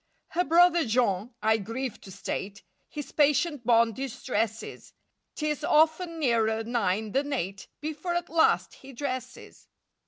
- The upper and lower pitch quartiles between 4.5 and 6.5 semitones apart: Yes, wide, 5.5 semitones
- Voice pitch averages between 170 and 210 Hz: No, very high, 255 Hz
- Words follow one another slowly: Yes, slow, 125 wpm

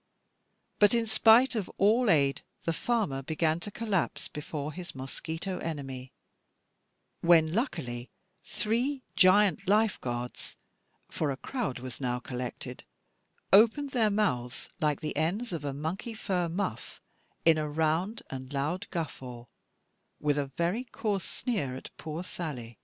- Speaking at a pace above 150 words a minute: No, slow, 135 wpm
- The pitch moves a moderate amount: No, wide, 7.0 semitones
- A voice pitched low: No, medium, 165 Hz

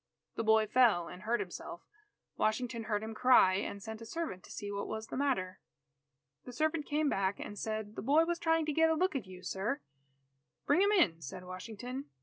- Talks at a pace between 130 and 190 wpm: No, fast, 205 wpm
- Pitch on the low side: No, high, 220 Hz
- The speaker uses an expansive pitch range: Yes, wide, 6.2 semitones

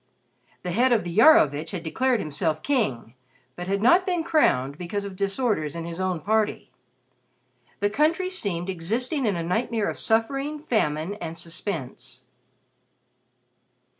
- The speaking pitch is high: Yes, high, 200 Hz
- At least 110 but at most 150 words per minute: Yes, average, 140 wpm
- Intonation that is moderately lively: No, wide, 7.0 semitones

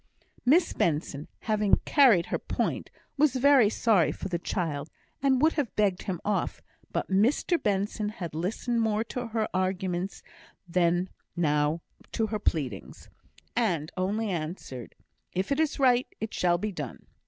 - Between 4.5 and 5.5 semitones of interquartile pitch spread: Yes, average, 5.0 semitones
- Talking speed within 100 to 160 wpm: Yes, average, 150 wpm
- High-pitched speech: Yes, high, 195 Hz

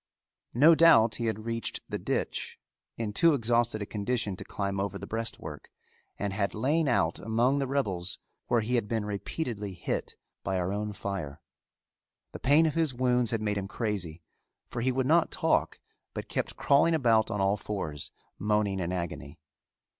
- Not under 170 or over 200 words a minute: Yes, average, 175 wpm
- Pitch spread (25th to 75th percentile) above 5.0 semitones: No, average, 4.1 semitones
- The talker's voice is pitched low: Yes, low, 110 Hz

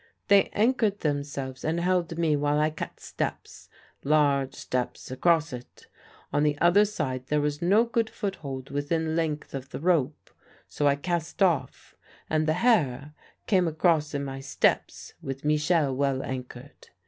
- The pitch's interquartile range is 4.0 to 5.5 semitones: No, average, 3.6 semitones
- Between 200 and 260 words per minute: No, average, 155 wpm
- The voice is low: No, medium, 150 Hz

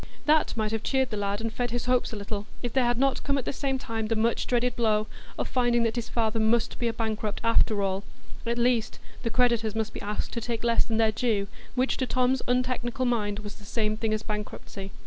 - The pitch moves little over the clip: Yes, narrow, 2.3 semitones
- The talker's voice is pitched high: Yes, high, 230 Hz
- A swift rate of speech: Yes, fast, 240 wpm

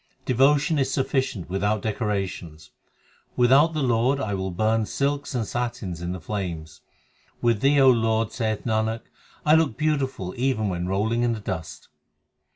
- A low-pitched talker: Yes, low, 115 Hz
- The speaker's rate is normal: Yes, average, 155 wpm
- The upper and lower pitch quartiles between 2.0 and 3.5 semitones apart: No, wide, 5.4 semitones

